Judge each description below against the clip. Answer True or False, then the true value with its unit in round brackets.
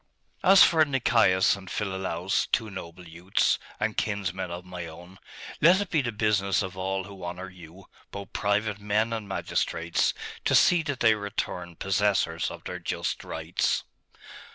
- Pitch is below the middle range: True (95 Hz)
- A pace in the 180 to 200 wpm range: False (155 wpm)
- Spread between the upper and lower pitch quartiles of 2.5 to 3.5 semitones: True (3.0 semitones)